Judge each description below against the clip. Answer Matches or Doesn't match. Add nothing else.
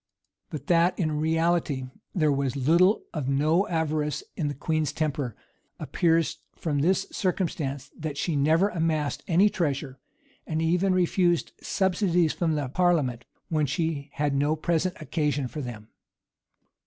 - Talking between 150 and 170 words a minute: Doesn't match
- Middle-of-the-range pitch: Matches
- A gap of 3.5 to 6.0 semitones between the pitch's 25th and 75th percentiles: Doesn't match